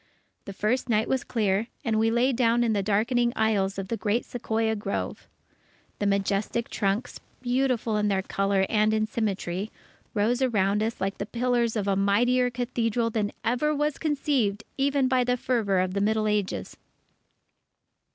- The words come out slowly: No, average, 160 wpm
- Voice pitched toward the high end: Yes, high, 220 Hz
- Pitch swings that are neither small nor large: Yes, average, 3.2 semitones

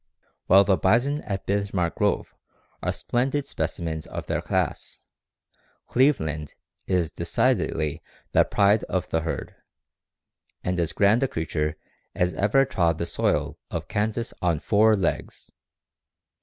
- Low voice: Yes, very low, 95 Hz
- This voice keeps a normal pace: No, slow, 130 wpm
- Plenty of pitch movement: No, average, 5.0 semitones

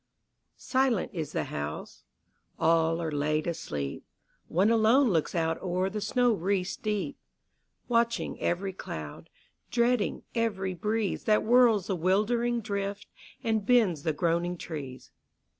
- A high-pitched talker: Yes, high, 195 Hz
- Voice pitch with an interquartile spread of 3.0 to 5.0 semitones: No, wide, 5.5 semitones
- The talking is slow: Yes, slow, 125 wpm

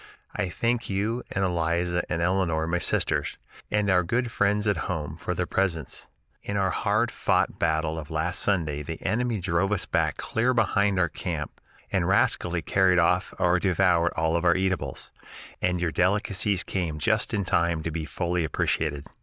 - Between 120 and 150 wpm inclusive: No, average, 170 wpm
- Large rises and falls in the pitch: No, average, 3.2 semitones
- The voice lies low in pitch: Yes, very low, 90 Hz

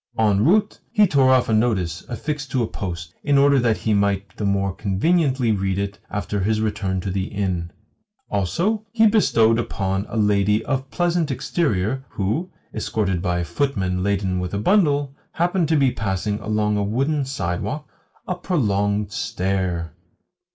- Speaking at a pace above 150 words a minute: Yes, average, 165 wpm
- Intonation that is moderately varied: No, wide, 6.3 semitones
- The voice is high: No, low, 105 Hz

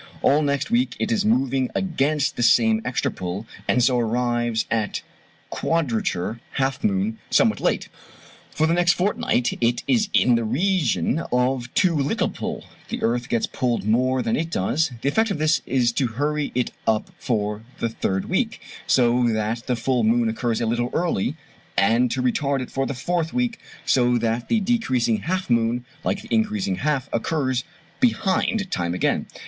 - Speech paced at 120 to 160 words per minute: No, average, 175 wpm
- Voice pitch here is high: No, low, 125 Hz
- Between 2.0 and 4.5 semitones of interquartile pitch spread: No, wide, 5.6 semitones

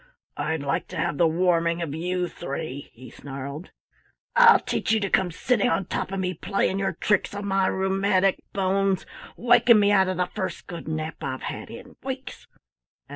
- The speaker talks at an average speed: Yes, average, 180 wpm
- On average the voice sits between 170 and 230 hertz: Yes, medium, 185 Hz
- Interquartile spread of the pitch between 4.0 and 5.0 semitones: No, average, 3.5 semitones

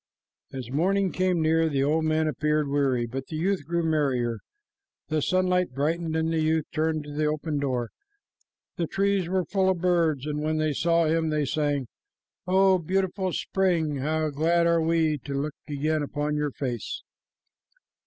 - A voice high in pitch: No, medium, 155 Hz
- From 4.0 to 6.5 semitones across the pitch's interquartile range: No, average, 2.7 semitones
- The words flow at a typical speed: Yes, average, 165 wpm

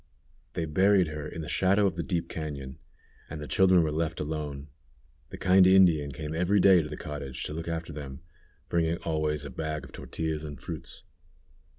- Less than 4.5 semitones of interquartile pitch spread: Yes, narrow, 2.5 semitones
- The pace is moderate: Yes, average, 190 wpm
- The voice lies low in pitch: Yes, very low, 80 Hz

